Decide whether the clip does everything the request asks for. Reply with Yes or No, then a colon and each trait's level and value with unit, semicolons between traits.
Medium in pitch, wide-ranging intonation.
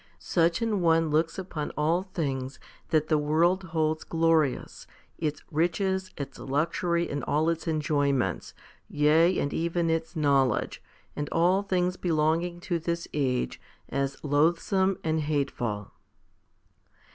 No: medium, 160 Hz; average, 2.7 semitones